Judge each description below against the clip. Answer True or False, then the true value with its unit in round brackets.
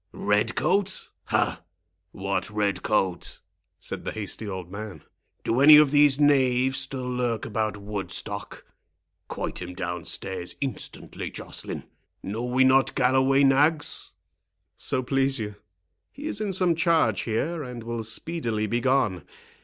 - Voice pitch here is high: False (125 Hz)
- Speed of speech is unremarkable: False (130 wpm)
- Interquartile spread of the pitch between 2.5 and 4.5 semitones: False (4.9 semitones)